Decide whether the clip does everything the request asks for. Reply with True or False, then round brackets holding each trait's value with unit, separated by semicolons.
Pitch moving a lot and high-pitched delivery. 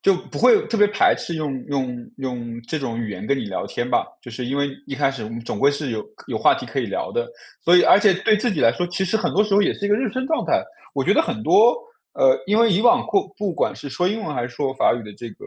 False (9.0 semitones; 155 Hz)